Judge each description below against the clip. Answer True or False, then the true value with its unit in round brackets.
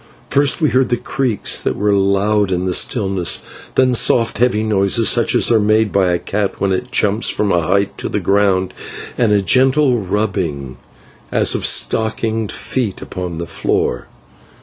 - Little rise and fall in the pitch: False (3.4 semitones)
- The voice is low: True (105 Hz)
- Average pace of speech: True (170 wpm)